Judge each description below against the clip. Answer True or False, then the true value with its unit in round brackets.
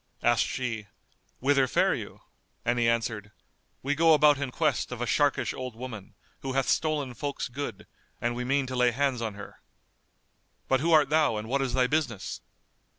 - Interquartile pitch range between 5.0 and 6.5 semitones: False (3.2 semitones)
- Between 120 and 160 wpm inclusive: False (185 wpm)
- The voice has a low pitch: True (130 Hz)